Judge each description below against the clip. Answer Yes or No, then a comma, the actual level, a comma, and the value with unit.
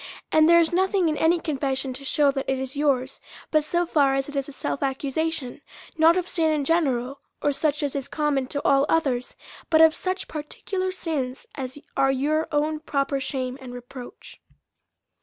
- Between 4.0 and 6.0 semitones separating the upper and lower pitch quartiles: No, average, 2.9 semitones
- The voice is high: Yes, very high, 290 Hz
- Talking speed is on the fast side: No, average, 190 wpm